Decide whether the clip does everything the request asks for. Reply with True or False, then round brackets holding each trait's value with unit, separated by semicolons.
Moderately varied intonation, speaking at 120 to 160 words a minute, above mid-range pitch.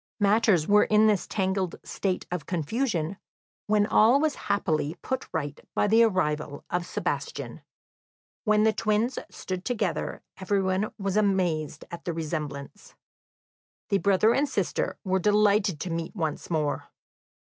True (4.1 semitones; 140 wpm; 195 Hz)